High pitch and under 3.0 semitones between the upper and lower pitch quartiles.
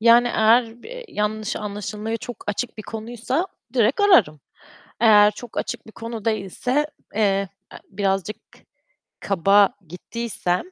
Yes: high, 220 Hz; narrow, 2.6 semitones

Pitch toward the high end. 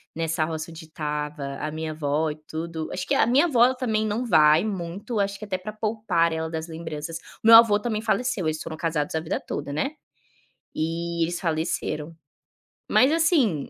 No: medium, 165 Hz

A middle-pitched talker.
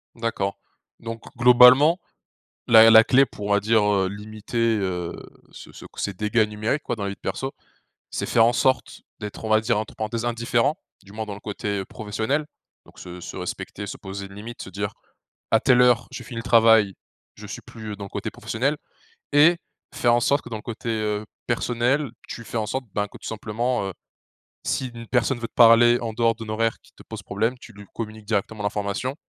No: low, 115 Hz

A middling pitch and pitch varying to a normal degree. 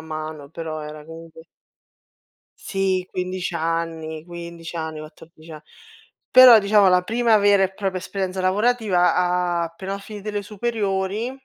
Yes: medium, 180 Hz; average, 3.5 semitones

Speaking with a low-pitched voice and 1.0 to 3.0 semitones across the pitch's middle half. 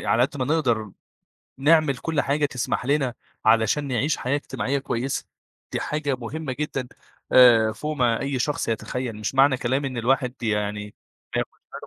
No: low, 130 Hz; average, 3.4 semitones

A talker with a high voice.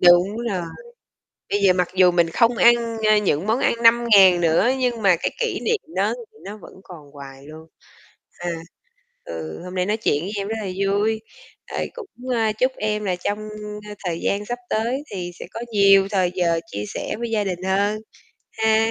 Yes: high, 200 Hz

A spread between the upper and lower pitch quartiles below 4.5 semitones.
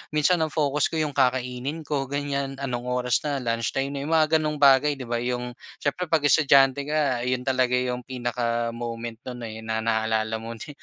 Yes: average, 3.1 semitones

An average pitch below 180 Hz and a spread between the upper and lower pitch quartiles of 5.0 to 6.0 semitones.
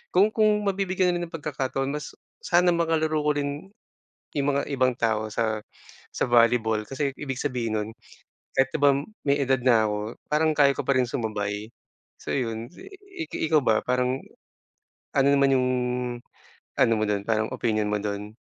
Yes: low, 135 Hz; wide, 5.4 semitones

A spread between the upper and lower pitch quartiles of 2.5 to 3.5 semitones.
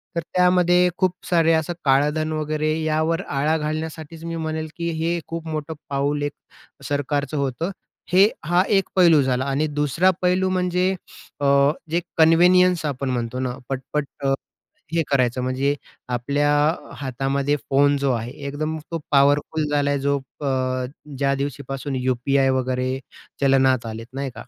Yes: average, 3.2 semitones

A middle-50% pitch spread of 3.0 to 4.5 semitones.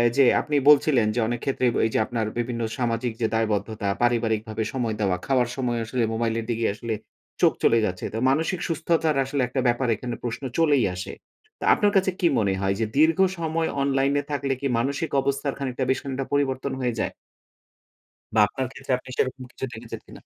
Yes: average, 3.5 semitones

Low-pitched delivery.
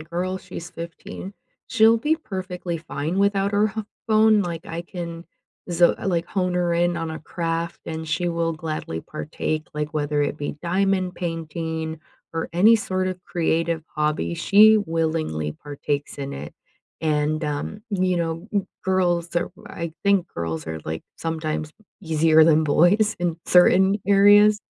No: medium, 170 Hz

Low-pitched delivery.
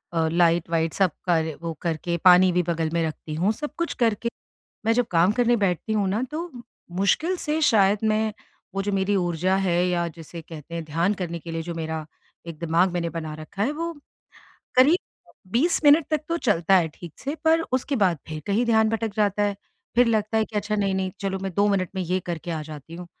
No: high, 190 Hz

